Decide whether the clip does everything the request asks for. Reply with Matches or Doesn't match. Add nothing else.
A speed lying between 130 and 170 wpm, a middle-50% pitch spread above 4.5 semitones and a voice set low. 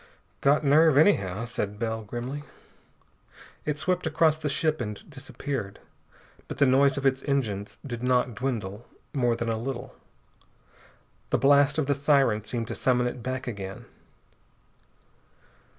Doesn't match